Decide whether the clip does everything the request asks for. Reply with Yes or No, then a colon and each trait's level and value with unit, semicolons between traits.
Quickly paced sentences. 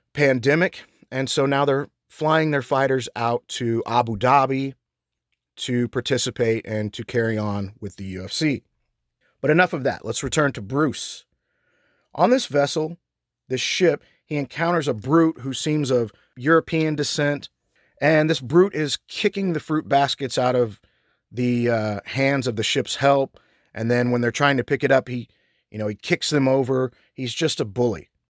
No: average, 170 wpm